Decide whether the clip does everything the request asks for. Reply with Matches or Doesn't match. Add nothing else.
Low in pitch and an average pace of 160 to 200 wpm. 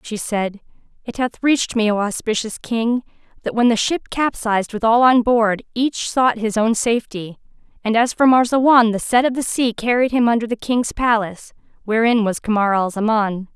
Doesn't match